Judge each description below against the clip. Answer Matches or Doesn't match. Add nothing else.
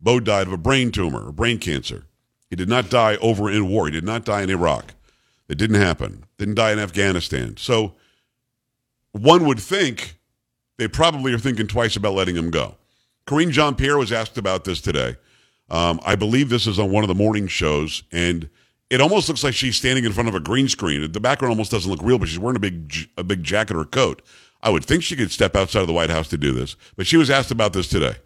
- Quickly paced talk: Matches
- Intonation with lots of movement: Doesn't match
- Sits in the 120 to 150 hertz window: Doesn't match